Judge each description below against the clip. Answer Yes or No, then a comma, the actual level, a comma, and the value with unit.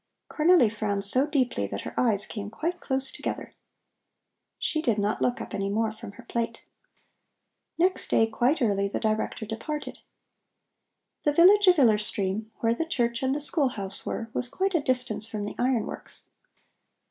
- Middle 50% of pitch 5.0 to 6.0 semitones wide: Yes, wide, 5.4 semitones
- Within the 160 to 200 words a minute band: Yes, average, 170 wpm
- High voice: Yes, high, 235 Hz